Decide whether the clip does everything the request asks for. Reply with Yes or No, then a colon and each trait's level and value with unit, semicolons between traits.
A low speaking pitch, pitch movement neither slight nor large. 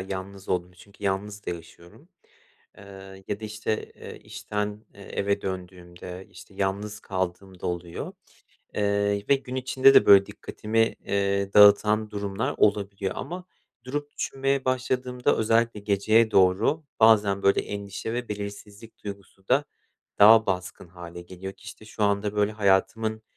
No: low, 100 Hz; narrow, 2.3 semitones